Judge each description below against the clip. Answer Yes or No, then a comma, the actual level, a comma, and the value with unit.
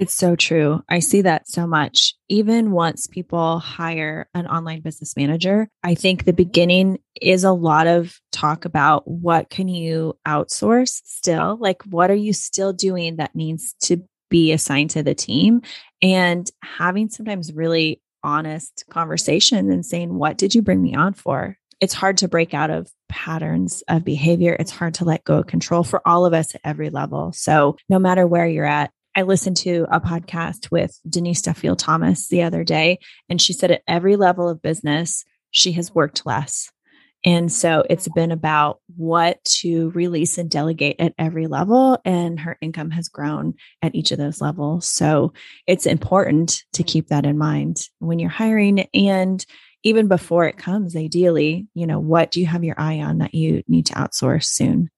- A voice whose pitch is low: No, medium, 170 Hz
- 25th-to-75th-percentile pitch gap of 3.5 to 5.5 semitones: No, average, 2.8 semitones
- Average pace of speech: Yes, average, 185 wpm